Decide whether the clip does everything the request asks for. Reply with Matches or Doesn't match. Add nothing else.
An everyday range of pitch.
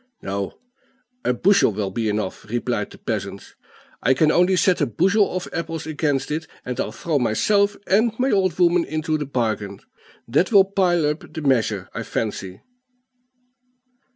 Doesn't match